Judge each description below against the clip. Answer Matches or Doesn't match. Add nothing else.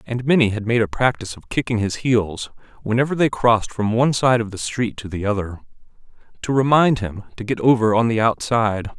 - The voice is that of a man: Matches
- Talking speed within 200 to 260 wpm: Matches